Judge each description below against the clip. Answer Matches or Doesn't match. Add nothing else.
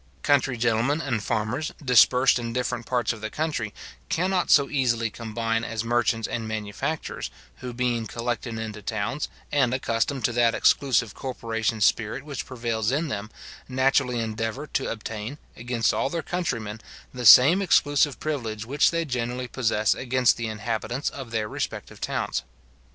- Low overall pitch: Matches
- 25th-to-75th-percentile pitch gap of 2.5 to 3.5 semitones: Matches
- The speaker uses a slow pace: Doesn't match